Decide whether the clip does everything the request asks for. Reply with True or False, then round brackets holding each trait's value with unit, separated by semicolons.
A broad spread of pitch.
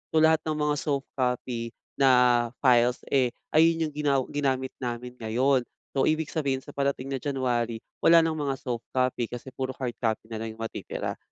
False (2.9 semitones)